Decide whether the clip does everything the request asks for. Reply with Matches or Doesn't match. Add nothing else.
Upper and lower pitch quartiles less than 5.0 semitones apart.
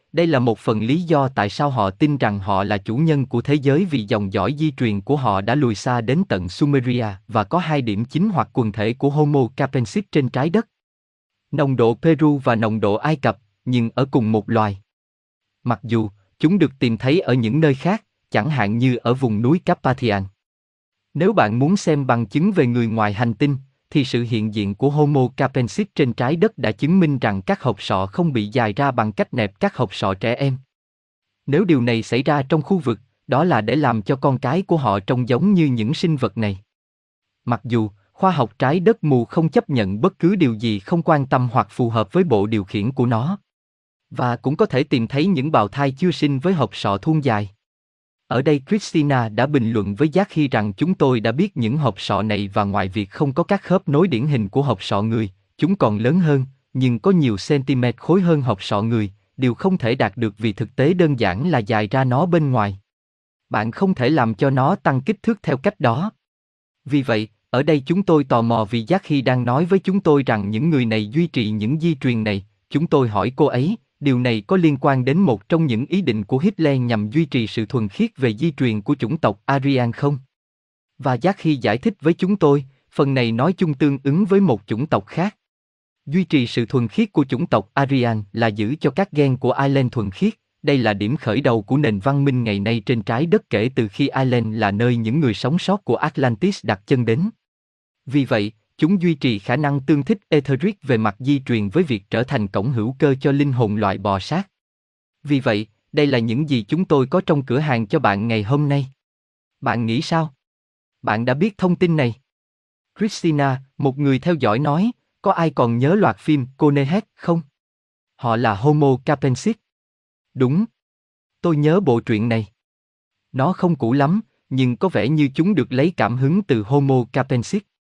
Doesn't match